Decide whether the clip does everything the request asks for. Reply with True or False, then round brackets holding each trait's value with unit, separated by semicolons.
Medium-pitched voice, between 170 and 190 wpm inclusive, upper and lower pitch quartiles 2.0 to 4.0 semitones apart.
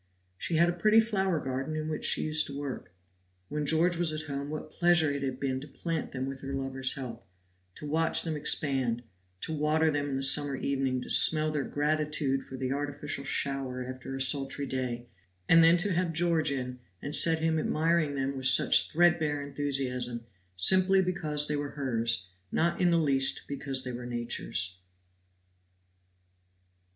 True (145 Hz; 180 wpm; 3.1 semitones)